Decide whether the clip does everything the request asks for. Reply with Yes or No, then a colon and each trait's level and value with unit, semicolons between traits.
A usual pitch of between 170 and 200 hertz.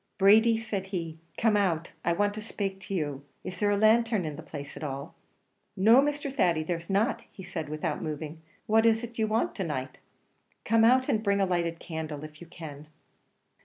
Yes: high, 190 Hz